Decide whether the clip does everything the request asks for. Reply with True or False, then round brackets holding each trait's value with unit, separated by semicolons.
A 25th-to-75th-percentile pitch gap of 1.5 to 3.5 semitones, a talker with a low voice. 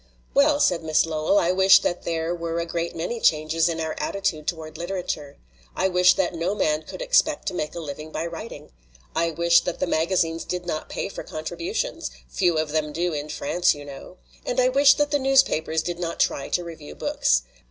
False (2.6 semitones; 170 Hz)